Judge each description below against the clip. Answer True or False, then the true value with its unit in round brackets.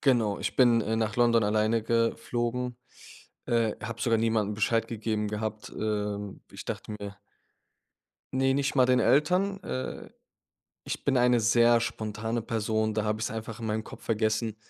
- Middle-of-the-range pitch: False (115 Hz)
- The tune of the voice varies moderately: False (1.8 semitones)